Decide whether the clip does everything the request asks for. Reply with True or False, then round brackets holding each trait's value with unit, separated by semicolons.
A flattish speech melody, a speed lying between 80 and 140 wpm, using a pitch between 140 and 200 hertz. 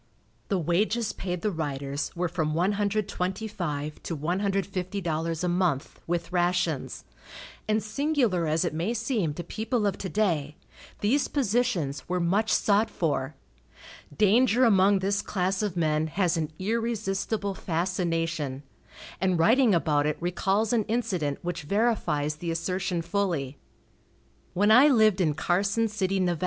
False (4.3 semitones; 135 wpm; 185 Hz)